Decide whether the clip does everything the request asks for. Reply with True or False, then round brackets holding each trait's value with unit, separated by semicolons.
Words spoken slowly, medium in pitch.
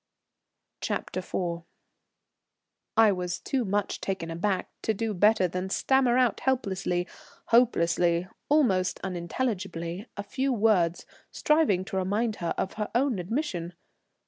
False (120 wpm; 195 Hz)